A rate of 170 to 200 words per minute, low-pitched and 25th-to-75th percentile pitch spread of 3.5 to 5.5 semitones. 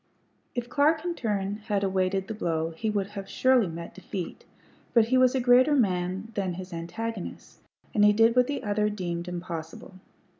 No: average, 180 wpm; high, 205 Hz; average, 4.4 semitones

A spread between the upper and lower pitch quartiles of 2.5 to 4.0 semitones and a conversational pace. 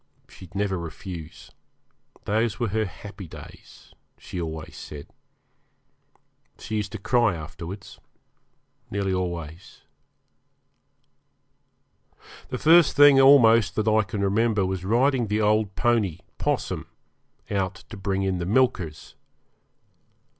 No: average, 3.4 semitones; slow, 110 wpm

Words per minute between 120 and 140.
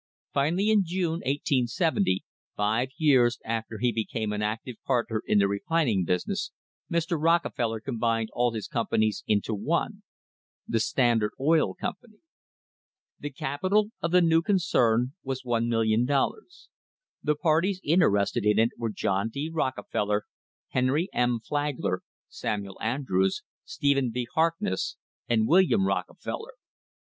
Yes: slow, 135 wpm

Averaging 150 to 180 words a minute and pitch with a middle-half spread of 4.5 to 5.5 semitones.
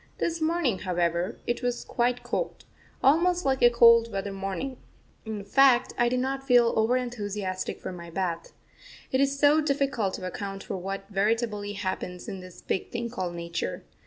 Yes: average, 170 wpm; average, 5.1 semitones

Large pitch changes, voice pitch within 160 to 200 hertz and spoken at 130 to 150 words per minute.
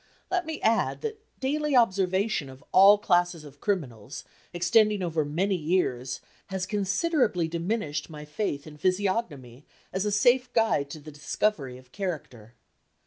Yes: wide, 6.3 semitones; medium, 185 Hz; average, 140 wpm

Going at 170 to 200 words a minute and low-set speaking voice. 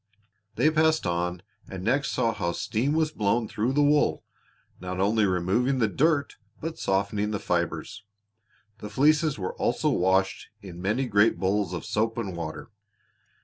No: average, 155 wpm; low, 105 Hz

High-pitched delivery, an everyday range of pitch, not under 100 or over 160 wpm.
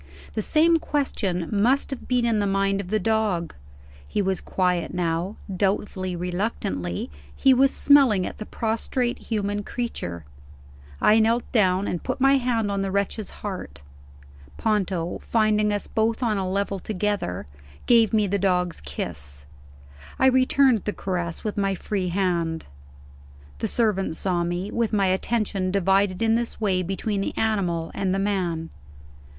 Yes: high, 200 Hz; average, 3.5 semitones; average, 155 wpm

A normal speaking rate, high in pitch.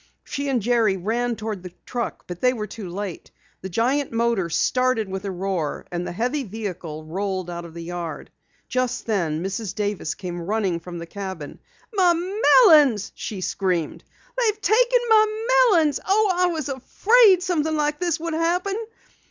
Yes: average, 170 wpm; high, 225 Hz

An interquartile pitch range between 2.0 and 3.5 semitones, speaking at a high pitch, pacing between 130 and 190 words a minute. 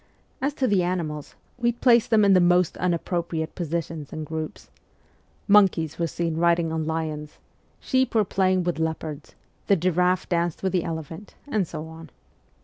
No: average, 2.9 semitones; medium, 170 Hz; average, 165 wpm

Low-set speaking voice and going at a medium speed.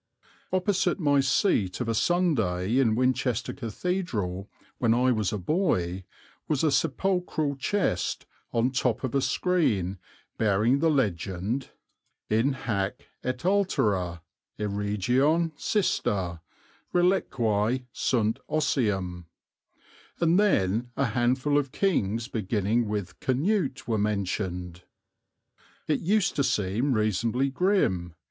No: low, 120 Hz; slow, 110 wpm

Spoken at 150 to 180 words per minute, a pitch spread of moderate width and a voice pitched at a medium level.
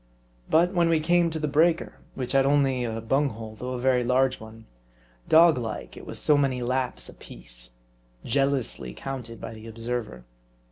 No: average, 175 wpm; average, 4.2 semitones; low, 130 Hz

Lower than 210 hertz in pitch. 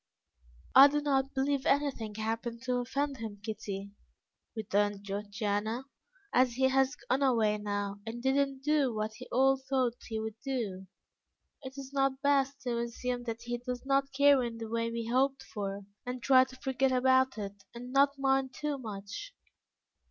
No: very high, 250 Hz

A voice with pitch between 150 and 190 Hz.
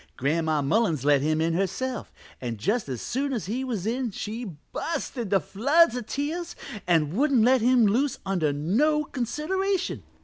No: high, 225 Hz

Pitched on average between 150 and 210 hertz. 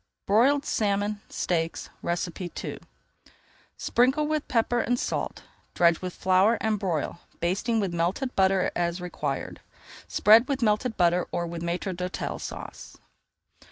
Yes: high, 190 Hz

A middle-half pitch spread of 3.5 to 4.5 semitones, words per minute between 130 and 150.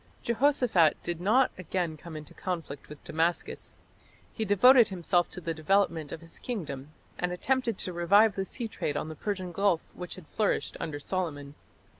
No: average, 4.2 semitones; average, 170 wpm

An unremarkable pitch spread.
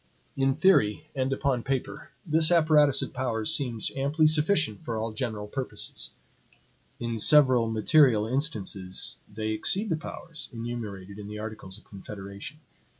No: wide, 5.7 semitones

